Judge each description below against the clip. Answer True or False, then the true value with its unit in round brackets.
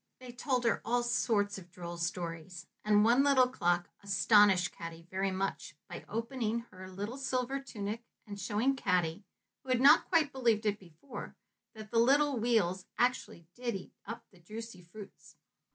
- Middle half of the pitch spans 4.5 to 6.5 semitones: True (4.8 semitones)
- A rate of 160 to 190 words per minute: True (165 wpm)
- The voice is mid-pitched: False (210 Hz)